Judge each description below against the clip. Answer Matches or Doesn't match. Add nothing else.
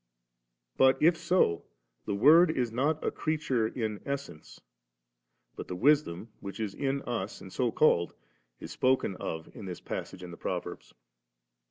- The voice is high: Doesn't match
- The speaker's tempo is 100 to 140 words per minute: Doesn't match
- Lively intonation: Matches